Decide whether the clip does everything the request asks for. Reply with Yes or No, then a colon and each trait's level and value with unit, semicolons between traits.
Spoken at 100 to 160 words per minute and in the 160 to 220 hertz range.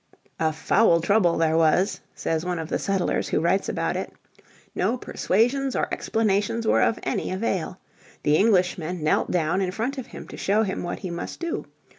No: average, 185 wpm; medium, 185 Hz